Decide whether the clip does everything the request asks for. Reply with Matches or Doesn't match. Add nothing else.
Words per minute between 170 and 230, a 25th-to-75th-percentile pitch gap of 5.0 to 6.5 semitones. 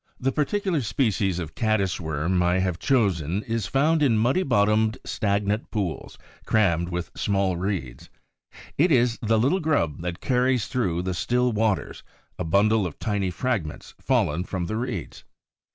Doesn't match